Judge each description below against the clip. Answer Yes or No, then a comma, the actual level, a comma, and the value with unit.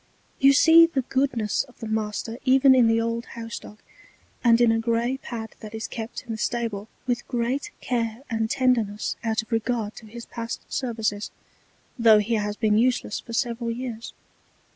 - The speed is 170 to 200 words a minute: Yes, average, 180 wpm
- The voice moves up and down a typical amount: No, narrow, 1.9 semitones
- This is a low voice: No, high, 230 Hz